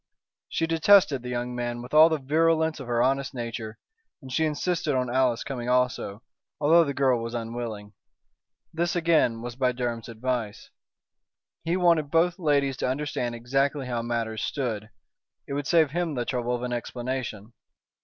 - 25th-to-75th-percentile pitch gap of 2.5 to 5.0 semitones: Yes, average, 4.2 semitones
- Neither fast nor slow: Yes, average, 165 wpm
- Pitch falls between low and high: No, low, 130 Hz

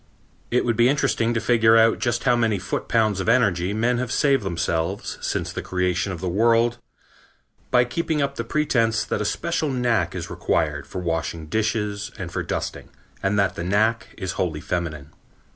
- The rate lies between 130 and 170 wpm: No, average, 185 wpm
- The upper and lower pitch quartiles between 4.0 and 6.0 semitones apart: Yes, average, 4.5 semitones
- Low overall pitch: Yes, low, 110 Hz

